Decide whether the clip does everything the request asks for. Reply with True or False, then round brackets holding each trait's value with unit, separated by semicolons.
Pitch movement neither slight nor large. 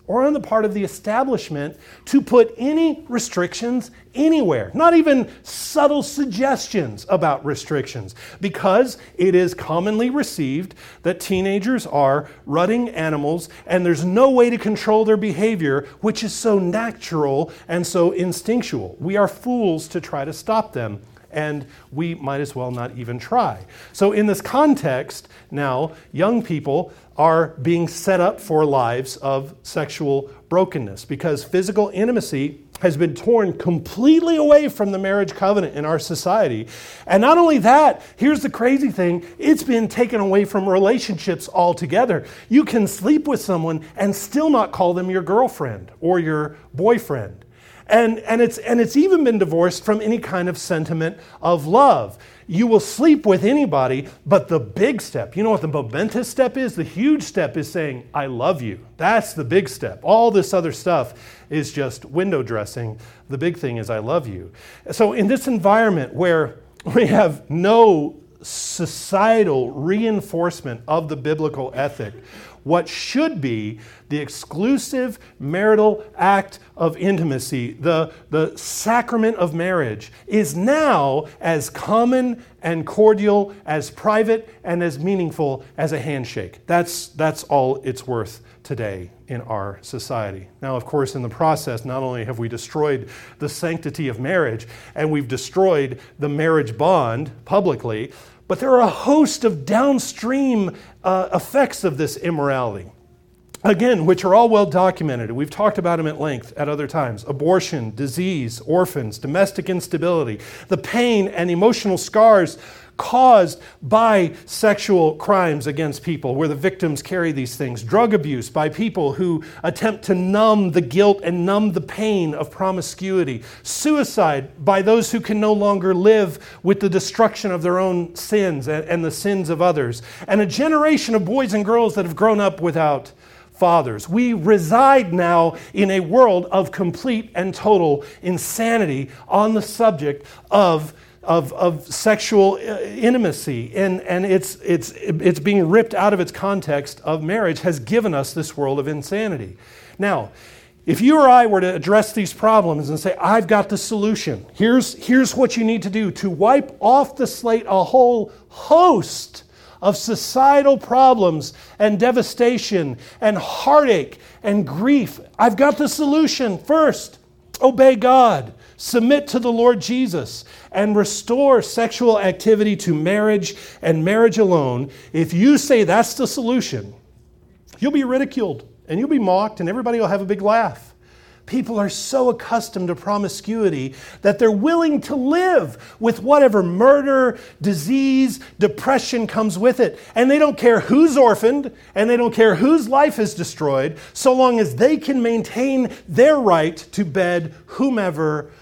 False (6.6 semitones)